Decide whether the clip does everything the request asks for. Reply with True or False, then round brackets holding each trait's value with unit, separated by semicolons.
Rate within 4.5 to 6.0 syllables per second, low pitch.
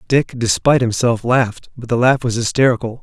True (5.8 syllables/s; 120 Hz)